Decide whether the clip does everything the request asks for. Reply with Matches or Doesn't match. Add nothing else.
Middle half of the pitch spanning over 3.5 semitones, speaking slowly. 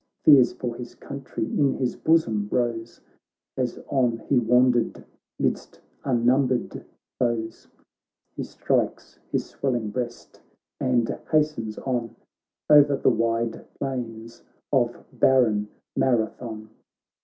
Doesn't match